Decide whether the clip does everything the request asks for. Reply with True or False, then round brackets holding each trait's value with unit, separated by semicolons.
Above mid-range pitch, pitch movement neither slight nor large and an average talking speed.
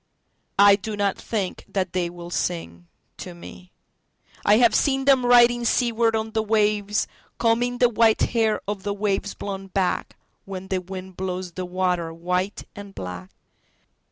True (200 Hz; 3.4 semitones; 145 wpm)